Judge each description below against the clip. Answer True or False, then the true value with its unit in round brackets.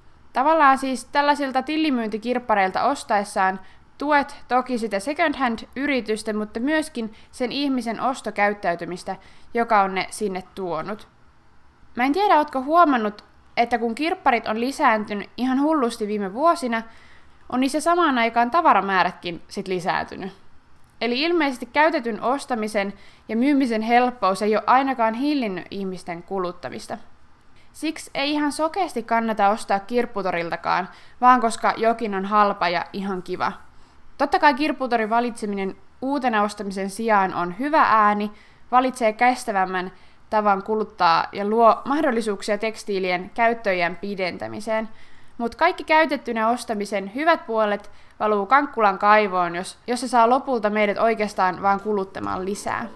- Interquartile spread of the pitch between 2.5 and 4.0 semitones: False (4.4 semitones)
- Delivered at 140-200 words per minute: False (120 wpm)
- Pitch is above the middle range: True (225 Hz)